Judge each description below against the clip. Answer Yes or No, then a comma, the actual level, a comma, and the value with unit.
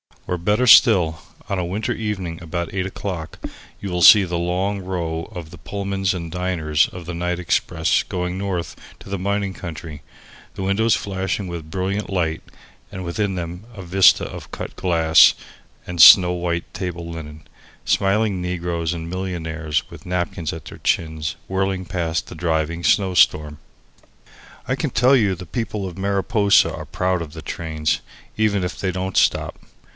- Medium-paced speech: Yes, average, 165 wpm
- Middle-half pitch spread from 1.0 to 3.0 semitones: Yes, narrow, 2.6 semitones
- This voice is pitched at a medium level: No, very low, 90 Hz